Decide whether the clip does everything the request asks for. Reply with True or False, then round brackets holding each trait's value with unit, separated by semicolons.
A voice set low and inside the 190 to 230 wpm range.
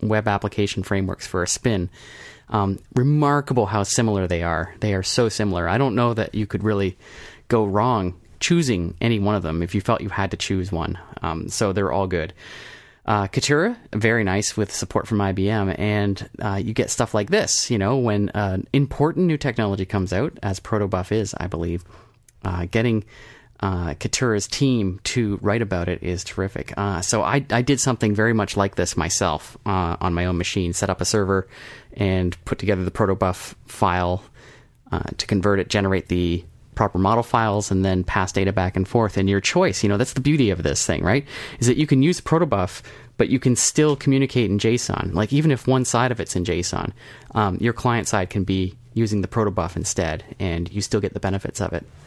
True (100 Hz; 205 wpm)